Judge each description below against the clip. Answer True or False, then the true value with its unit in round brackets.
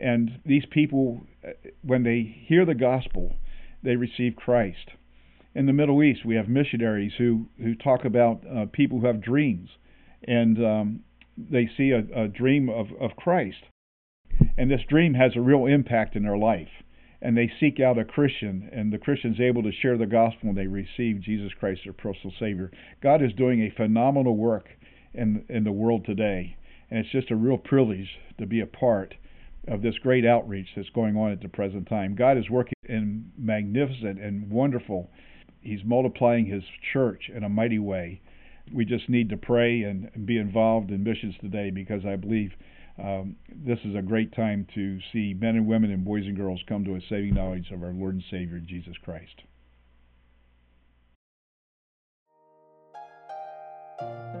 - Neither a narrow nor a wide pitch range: True (3.9 semitones)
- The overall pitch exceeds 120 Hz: False (110 Hz)